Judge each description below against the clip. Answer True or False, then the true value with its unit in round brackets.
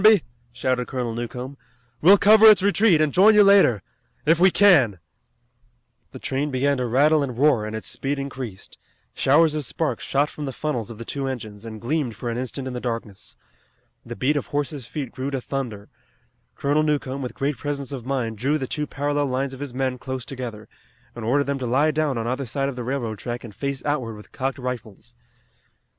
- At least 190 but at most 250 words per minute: True (205 wpm)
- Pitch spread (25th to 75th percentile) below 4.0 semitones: True (3.3 semitones)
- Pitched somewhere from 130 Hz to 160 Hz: True (135 Hz)